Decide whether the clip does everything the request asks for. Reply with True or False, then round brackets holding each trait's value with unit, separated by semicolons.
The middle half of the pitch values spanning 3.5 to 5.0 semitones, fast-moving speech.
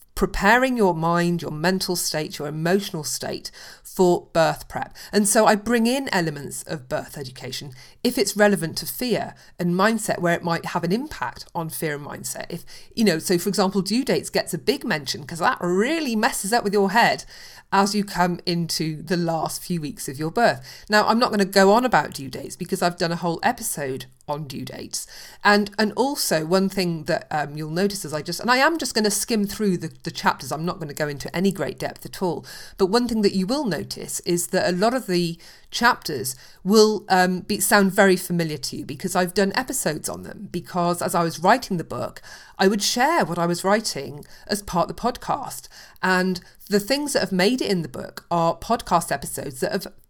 True (3.8 semitones; 220 wpm)